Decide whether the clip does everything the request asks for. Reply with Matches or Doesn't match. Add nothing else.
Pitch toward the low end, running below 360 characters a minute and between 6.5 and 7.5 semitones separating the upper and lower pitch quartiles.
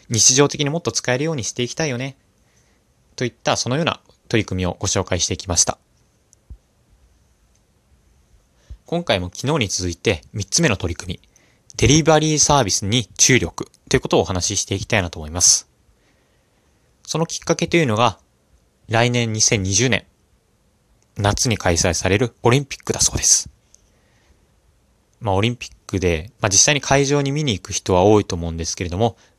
Doesn't match